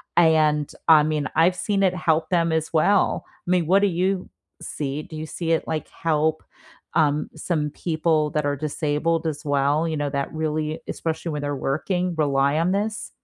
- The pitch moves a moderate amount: No, narrow, 2.2 semitones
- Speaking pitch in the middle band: Yes, medium, 155 Hz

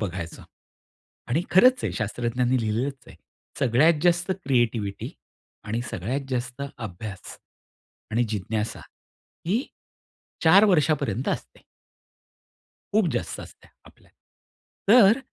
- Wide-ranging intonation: Yes, wide, 7.2 semitones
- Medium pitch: No, low, 125 Hz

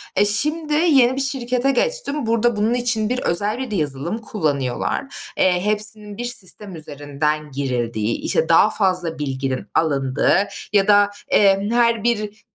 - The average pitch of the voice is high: Yes, high, 205 Hz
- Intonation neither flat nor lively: No, wide, 7.8 semitones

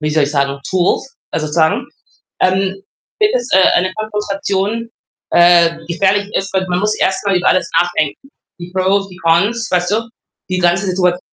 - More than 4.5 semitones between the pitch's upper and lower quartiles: No, narrow, 2.6 semitones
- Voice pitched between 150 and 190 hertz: Yes, medium, 185 Hz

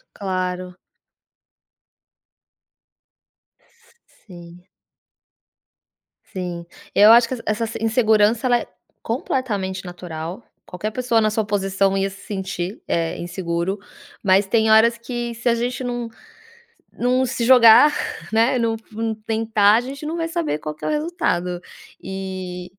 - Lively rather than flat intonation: No, average, 4.3 semitones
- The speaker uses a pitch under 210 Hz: No, high, 215 Hz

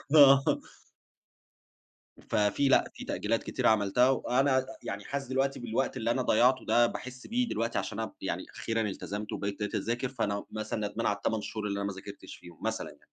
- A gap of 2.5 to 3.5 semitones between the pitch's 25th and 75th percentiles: No, average, 4.1 semitones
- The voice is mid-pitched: No, low, 115 Hz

